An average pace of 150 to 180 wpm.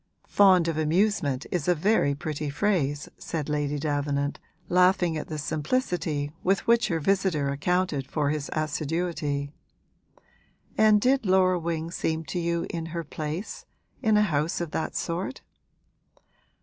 No: average, 140 wpm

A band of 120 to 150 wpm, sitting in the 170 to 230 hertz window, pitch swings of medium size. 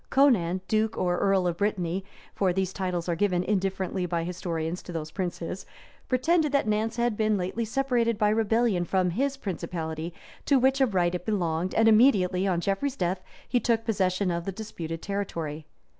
No: average, 175 wpm; high, 190 Hz; average, 4.1 semitones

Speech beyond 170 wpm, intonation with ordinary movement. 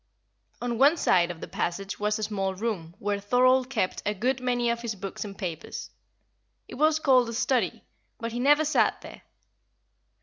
Yes: average, 180 wpm; average, 4.4 semitones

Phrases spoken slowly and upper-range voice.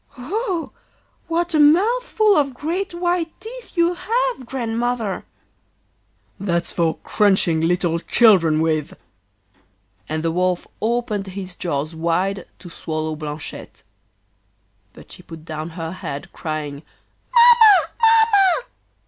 Yes: slow, 115 wpm; high, 210 Hz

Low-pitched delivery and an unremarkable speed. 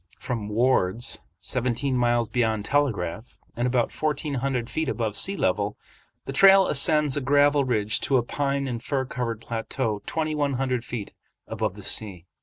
Yes: low, 125 Hz; average, 165 wpm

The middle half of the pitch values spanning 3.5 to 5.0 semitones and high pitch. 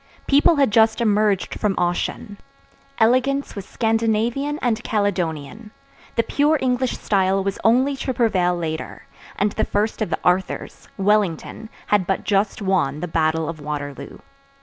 Yes: average, 4.5 semitones; high, 205 Hz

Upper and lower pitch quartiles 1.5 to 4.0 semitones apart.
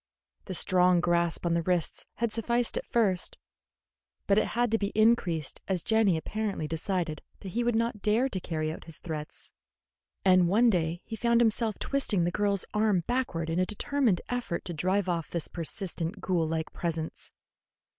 No: average, 4.7 semitones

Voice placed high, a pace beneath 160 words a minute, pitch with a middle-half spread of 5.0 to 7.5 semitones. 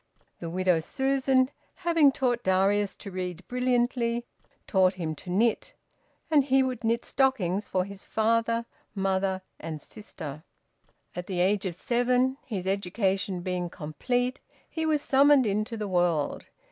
Yes: high, 210 Hz; average, 140 wpm; average, 5.3 semitones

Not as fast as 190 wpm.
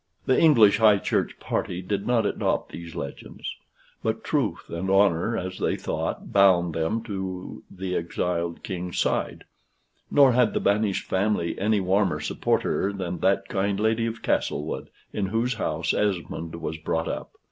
Yes: average, 155 wpm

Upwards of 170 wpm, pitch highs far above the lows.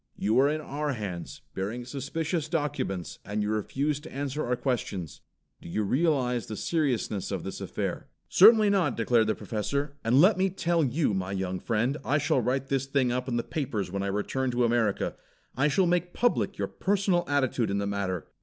Yes: average, 195 wpm; wide, 6.0 semitones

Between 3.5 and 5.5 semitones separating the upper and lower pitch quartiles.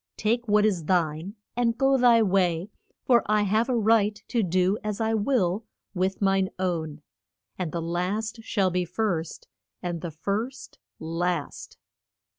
Yes: average, 4.0 semitones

